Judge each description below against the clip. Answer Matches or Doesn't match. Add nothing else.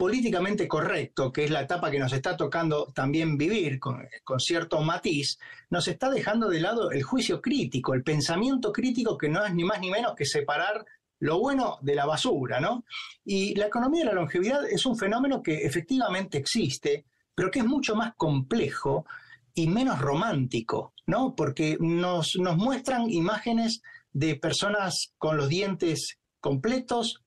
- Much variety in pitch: Matches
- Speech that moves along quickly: Doesn't match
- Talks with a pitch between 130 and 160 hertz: Doesn't match